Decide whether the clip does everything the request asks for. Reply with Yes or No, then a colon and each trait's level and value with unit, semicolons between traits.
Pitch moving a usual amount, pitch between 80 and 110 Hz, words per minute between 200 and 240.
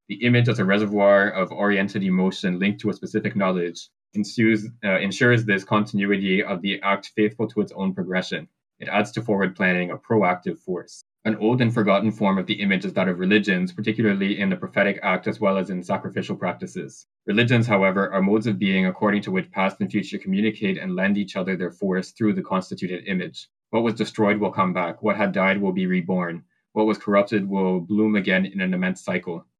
No: narrow, 2.2 semitones; low, 100 Hz; fast, 205 wpm